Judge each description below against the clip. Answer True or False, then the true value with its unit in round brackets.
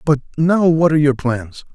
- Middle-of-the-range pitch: True (150 Hz)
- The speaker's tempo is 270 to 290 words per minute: False (205 wpm)